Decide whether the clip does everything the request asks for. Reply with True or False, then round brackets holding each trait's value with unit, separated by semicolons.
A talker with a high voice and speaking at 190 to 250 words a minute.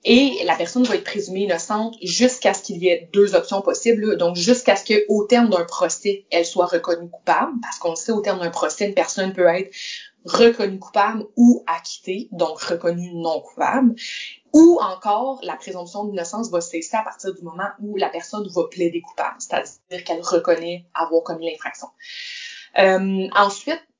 False (195 Hz; 180 wpm)